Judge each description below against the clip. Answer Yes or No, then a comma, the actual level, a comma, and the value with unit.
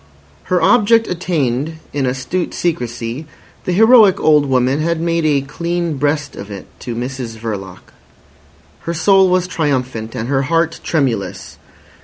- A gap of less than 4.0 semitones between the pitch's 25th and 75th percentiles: No, wide, 5.4 semitones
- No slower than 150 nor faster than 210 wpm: No, average, 140 wpm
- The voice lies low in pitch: No, medium, 150 Hz